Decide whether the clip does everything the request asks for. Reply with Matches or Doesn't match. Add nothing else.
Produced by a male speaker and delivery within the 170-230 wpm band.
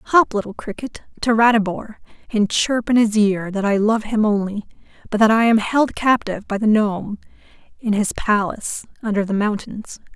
Doesn't match